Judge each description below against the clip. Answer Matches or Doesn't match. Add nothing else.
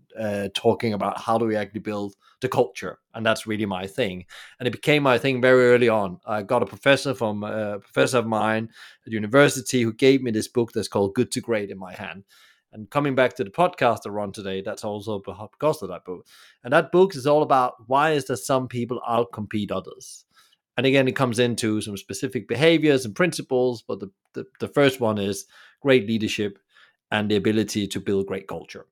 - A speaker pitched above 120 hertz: Doesn't match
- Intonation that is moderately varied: Matches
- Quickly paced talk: Matches